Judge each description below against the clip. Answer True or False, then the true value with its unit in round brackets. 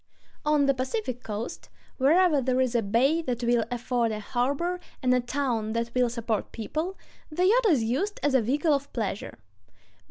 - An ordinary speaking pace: True (180 wpm)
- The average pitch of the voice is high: True (255 Hz)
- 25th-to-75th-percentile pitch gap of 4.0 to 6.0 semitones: True (4.3 semitones)